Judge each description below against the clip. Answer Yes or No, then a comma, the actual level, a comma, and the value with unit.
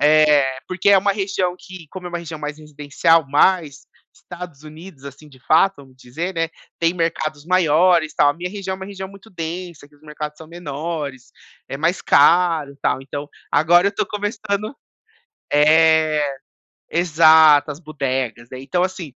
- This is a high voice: No, medium, 160 Hz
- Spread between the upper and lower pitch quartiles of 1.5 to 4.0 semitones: Yes, average, 3.5 semitones